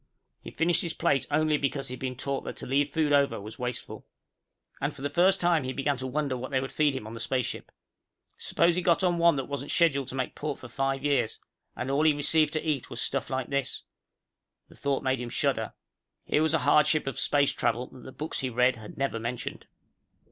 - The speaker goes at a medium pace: No, fast, 230 wpm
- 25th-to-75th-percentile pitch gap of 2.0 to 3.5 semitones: Yes, average, 2.8 semitones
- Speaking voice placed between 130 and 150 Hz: Yes, medium, 140 Hz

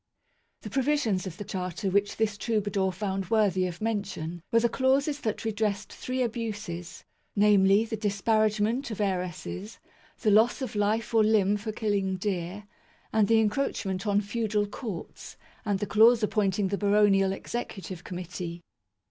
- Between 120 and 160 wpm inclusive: Yes, average, 150 wpm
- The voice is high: Yes, high, 205 Hz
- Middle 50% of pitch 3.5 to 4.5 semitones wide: No, narrow, 2.5 semitones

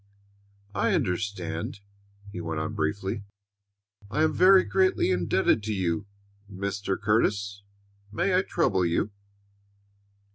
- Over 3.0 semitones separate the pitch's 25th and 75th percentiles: Yes, average, 3.4 semitones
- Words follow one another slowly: Yes, slow, 110 wpm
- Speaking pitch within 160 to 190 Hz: No, low, 100 Hz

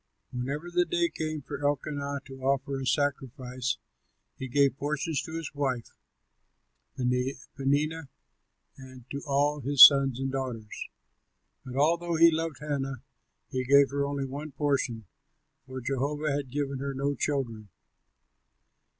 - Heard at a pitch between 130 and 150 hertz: Yes, medium, 140 Hz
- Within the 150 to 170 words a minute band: No, slow, 135 wpm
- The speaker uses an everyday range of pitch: No, narrow, 1.9 semitones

